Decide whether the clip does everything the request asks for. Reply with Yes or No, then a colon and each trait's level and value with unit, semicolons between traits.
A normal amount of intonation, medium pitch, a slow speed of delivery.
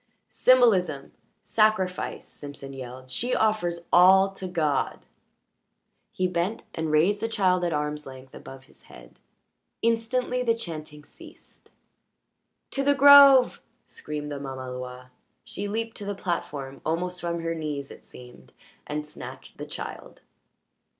No: wide, 6.8 semitones; medium, 170 Hz; slow, 130 wpm